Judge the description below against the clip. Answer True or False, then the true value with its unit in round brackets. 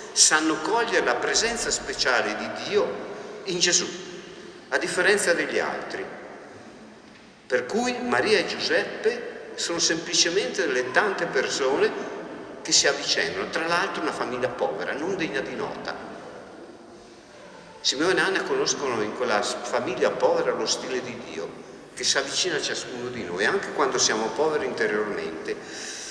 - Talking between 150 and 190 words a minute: False (135 wpm)